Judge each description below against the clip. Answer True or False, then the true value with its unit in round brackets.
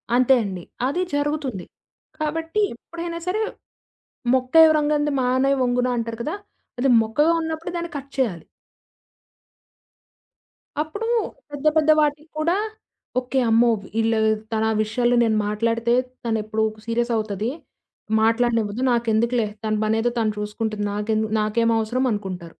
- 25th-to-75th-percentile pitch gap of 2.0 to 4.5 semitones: False (5.1 semitones)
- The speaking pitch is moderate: False (240 Hz)